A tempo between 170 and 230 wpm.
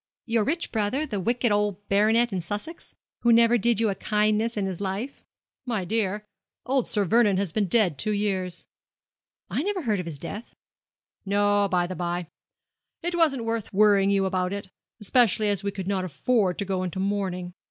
Yes: average, 190 wpm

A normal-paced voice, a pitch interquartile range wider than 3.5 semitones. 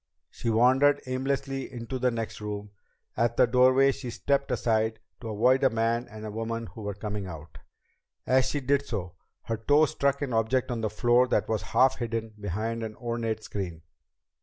No: average, 180 wpm; average, 3.0 semitones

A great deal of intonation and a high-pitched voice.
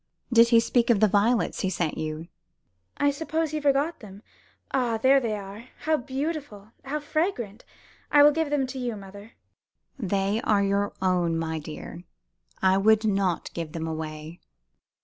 Yes: wide, 6.2 semitones; high, 215 Hz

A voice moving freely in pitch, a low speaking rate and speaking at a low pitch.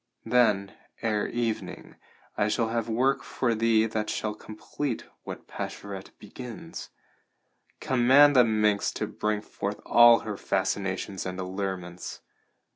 No: average, 3.0 semitones; slow, 120 wpm; low, 110 Hz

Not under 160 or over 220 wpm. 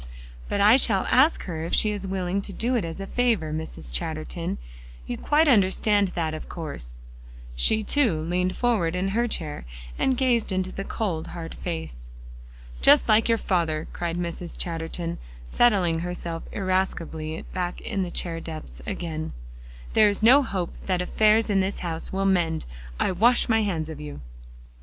Yes: average, 170 wpm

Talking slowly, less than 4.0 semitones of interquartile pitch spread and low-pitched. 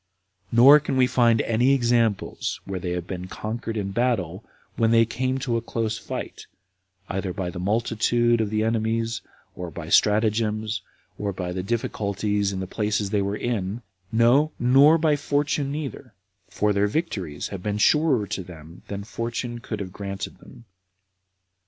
No: average, 165 wpm; average, 3.3 semitones; low, 110 Hz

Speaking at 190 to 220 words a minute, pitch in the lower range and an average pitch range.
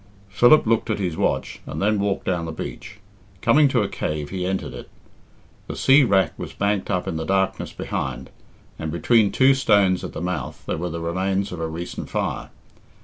Yes: average, 200 wpm; very low, 95 Hz; average, 3.6 semitones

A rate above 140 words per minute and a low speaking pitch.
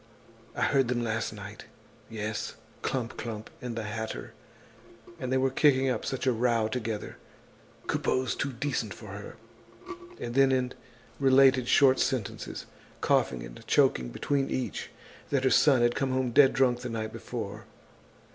Yes: average, 155 wpm; low, 125 Hz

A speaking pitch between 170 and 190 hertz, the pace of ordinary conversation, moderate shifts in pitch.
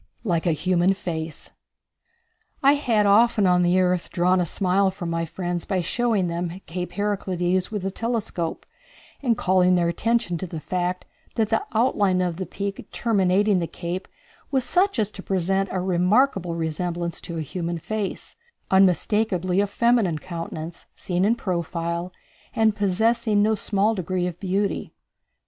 Yes: medium, 185 Hz; average, 155 wpm; average, 3.0 semitones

